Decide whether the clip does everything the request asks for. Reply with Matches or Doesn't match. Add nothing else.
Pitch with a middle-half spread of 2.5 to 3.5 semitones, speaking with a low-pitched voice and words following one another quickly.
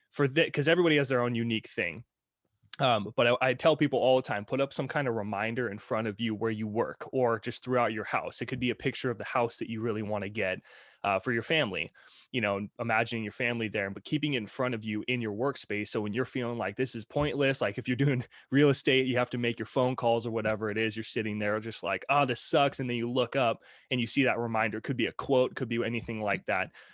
Matches